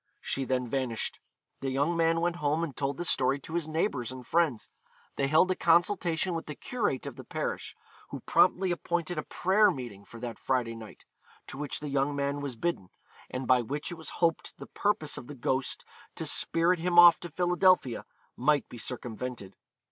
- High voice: No, medium, 145 Hz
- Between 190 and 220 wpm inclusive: Yes, average, 195 wpm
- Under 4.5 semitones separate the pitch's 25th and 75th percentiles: No, average, 5.0 semitones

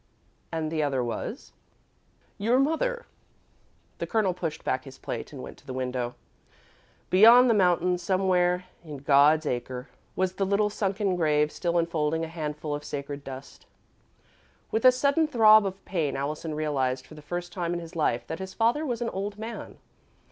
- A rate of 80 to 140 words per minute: No, average, 175 wpm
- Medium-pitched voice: Yes, medium, 170 Hz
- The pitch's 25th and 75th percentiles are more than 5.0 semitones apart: Yes, wide, 5.5 semitones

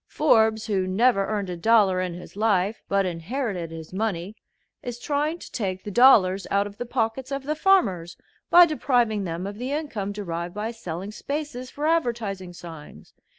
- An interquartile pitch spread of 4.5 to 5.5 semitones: Yes, average, 5.2 semitones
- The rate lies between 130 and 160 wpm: No, average, 175 wpm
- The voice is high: Yes, high, 210 Hz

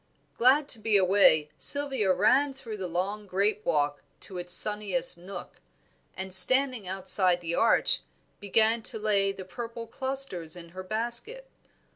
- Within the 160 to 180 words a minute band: No, average, 145 wpm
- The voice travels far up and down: No, average, 4.3 semitones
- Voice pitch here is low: No, high, 205 Hz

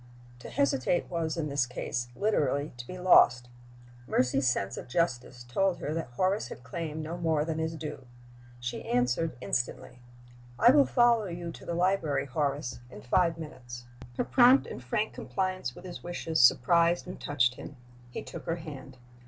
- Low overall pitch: No, medium, 155 Hz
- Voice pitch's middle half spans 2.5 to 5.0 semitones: No, wide, 5.6 semitones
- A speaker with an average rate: Yes, average, 170 wpm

